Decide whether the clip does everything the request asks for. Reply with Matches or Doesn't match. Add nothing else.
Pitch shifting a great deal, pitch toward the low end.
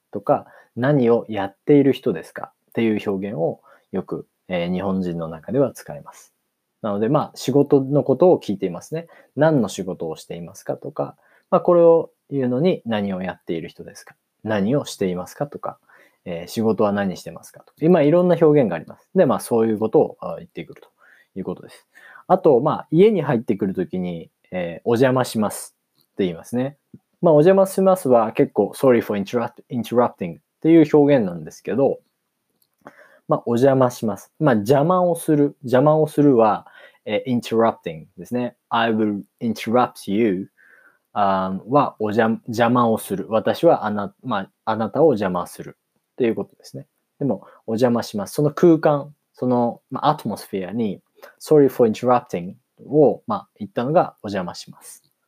Matches